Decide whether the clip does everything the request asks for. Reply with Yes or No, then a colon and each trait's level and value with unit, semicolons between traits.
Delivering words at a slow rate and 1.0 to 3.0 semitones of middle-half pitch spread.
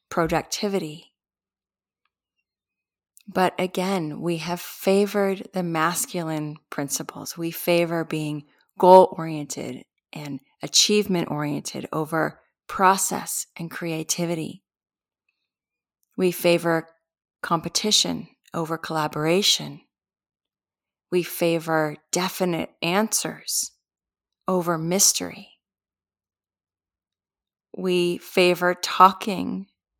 No: slow, 70 wpm; average, 3.5 semitones